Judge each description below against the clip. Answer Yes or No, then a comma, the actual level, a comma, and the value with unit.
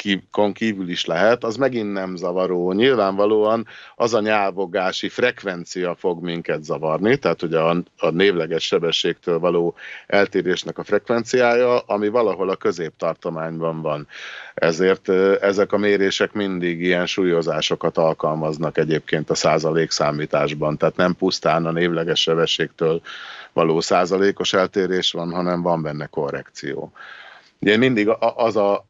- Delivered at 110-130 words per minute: Yes, average, 125 wpm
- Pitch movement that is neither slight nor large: Yes, average, 3.3 semitones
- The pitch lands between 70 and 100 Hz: Yes, very low, 90 Hz